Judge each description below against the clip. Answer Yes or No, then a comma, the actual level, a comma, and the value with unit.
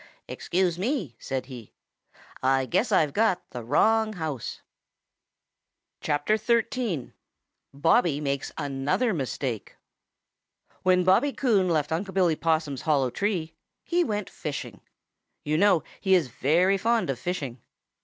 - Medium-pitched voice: Yes, medium, 165 Hz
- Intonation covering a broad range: Yes, wide, 6.6 semitones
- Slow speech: Yes, slow, 120 wpm